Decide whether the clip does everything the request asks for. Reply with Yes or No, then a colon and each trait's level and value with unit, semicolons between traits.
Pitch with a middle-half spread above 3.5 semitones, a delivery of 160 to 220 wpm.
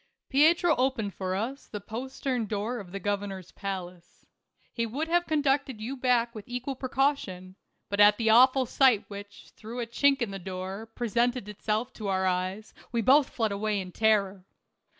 Yes: average, 4.5 semitones; average, 175 wpm